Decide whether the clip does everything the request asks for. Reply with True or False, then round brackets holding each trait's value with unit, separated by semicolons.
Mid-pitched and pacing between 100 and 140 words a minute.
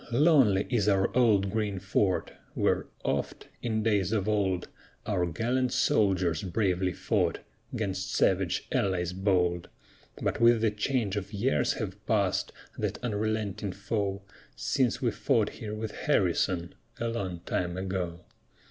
False (100 Hz; 135 wpm)